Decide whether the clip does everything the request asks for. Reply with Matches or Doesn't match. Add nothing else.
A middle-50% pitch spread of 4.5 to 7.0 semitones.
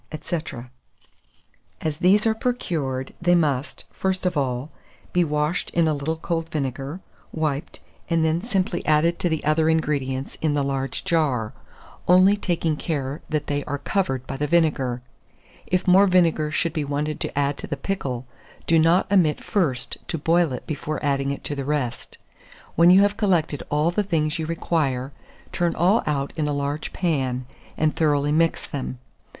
Doesn't match